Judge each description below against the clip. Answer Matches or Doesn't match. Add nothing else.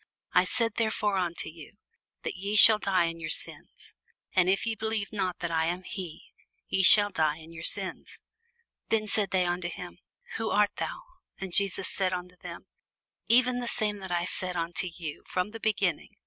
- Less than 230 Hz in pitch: Matches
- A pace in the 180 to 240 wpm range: Matches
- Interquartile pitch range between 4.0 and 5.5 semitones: Doesn't match